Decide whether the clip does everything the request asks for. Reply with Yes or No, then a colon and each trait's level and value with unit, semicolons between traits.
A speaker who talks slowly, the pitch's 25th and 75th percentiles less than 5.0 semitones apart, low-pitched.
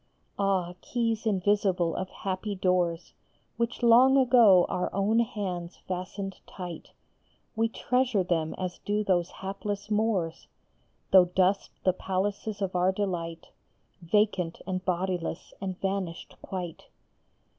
No: slow, 120 wpm; average, 2.7 semitones; high, 190 Hz